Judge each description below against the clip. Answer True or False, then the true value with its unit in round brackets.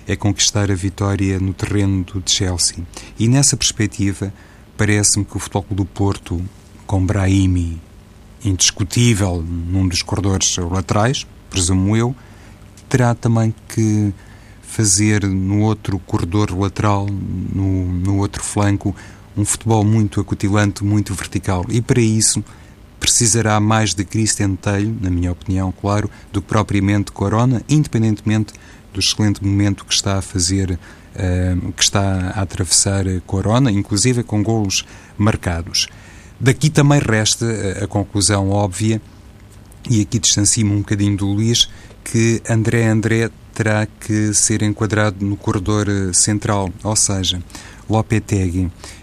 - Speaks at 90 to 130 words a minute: True (125 wpm)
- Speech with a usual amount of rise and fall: False (1.9 semitones)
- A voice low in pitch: True (100 Hz)